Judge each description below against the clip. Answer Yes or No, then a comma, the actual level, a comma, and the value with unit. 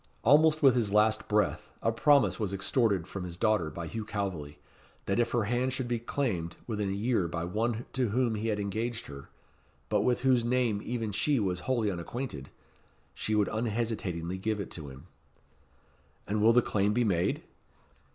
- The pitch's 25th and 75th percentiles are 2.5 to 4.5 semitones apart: Yes, average, 3.7 semitones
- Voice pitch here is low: Yes, low, 110 Hz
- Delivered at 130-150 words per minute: No, average, 180 wpm